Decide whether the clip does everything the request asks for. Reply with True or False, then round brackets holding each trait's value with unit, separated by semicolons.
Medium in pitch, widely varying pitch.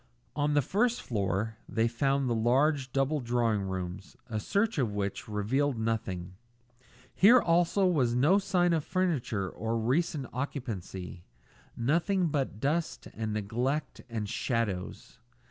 False (125 Hz; 6.1 semitones)